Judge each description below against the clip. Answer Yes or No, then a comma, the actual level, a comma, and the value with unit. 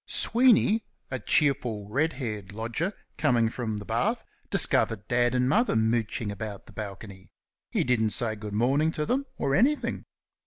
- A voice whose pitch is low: Yes, low, 120 Hz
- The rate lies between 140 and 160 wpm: Yes, average, 155 wpm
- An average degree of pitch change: No, wide, 5.7 semitones